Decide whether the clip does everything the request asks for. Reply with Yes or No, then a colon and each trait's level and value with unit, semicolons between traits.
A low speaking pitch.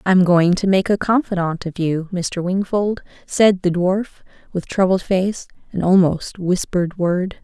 No: medium, 185 Hz